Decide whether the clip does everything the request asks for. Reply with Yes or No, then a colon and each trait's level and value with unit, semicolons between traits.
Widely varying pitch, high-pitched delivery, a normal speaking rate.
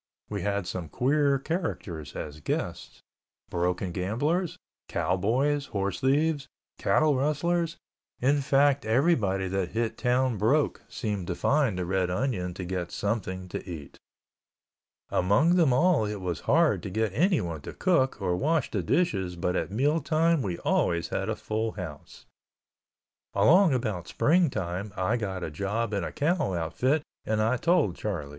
No: wide, 7.8 semitones; low, 110 Hz; average, 155 wpm